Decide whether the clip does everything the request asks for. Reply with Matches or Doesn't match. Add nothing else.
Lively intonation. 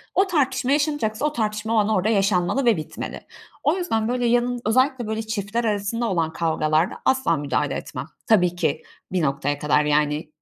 Matches